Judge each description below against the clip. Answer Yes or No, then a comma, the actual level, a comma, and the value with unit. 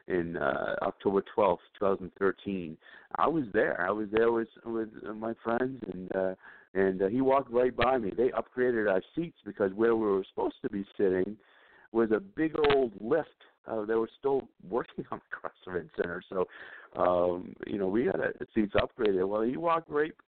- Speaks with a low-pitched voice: Yes, low, 110 Hz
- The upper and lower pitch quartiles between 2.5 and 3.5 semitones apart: No, average, 4.4 semitones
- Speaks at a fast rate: No, average, 195 wpm